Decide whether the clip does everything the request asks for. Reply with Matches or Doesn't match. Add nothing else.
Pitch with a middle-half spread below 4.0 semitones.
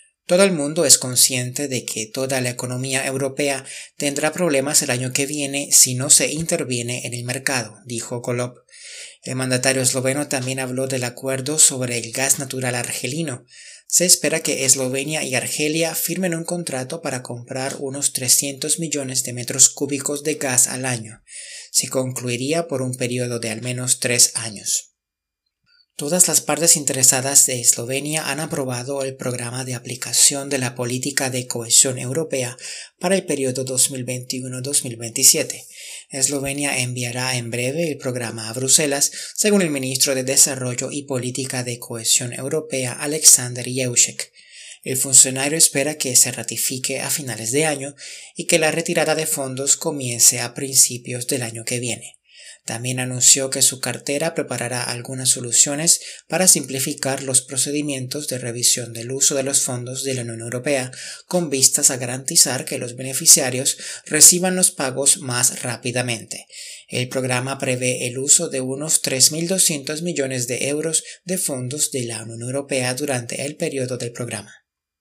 Matches